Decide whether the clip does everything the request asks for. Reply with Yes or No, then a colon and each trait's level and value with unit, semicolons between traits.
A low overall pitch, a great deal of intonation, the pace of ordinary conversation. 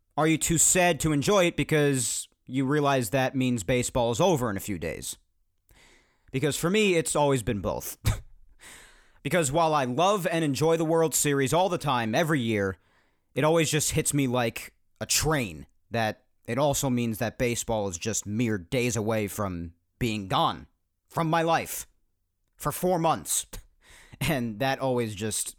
Yes: low, 130 Hz; wide, 6.5 semitones; average, 170 wpm